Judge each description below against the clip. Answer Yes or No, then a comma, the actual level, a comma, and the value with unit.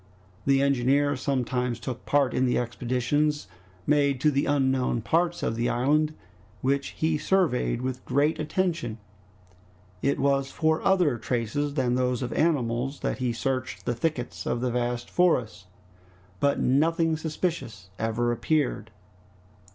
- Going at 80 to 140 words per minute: Yes, slow, 135 wpm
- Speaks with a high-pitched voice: No, low, 135 Hz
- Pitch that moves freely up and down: No, average, 3.6 semitones